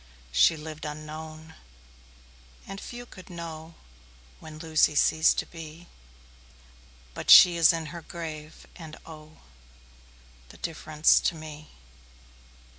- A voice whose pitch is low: No, medium, 160 Hz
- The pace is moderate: No, slow, 115 wpm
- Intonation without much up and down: Yes, narrow, 1.4 semitones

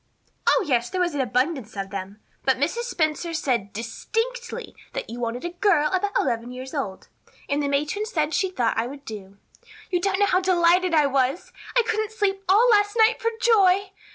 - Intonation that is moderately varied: No, wide, 7.9 semitones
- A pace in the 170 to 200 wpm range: Yes, average, 195 wpm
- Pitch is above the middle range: Yes, very high, 320 Hz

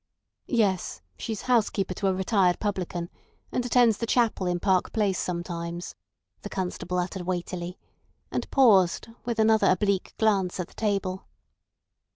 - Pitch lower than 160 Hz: No, high, 190 Hz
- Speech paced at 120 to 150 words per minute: Yes, average, 140 wpm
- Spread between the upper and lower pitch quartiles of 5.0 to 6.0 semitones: No, average, 3.4 semitones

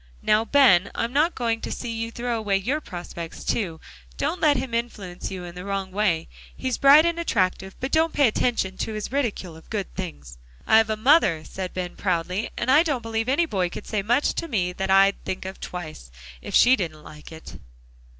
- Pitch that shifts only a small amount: No, wide, 5.5 semitones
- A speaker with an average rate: No, fast, 210 wpm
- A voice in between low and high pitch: No, high, 210 Hz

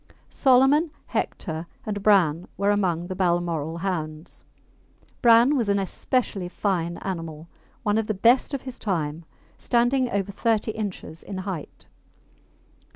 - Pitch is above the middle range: Yes, high, 195 Hz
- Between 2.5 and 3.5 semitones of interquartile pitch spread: No, average, 5.0 semitones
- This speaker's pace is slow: Yes, slow, 130 wpm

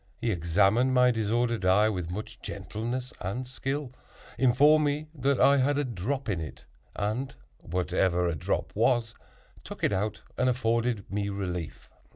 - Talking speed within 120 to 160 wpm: Yes, average, 155 wpm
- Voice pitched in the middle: No, low, 115 Hz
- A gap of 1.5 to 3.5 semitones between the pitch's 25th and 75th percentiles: No, average, 4.9 semitones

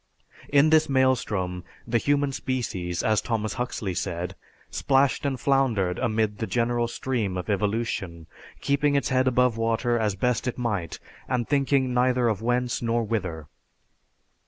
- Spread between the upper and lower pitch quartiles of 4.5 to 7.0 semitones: No, average, 3.8 semitones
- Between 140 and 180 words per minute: Yes, average, 145 wpm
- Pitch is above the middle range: No, low, 120 Hz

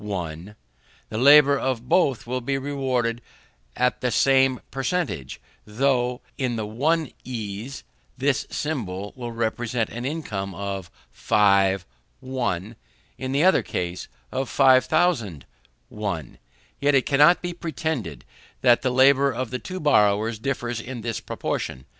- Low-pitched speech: Yes, low, 125 Hz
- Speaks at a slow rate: Yes, slow, 130 wpm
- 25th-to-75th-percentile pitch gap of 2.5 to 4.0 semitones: No, average, 4.7 semitones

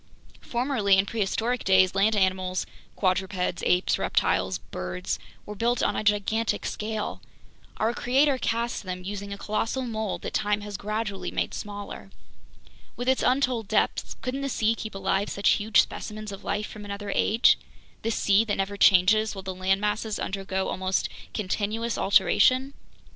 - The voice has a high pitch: Yes, high, 205 Hz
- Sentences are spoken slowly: No, average, 155 wpm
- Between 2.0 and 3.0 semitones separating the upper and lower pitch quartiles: Yes, average, 2.7 semitones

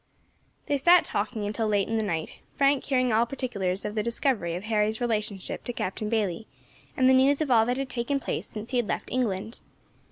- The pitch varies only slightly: No, average, 3.6 semitones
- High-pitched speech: Yes, high, 225 Hz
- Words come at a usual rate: No, fast, 210 wpm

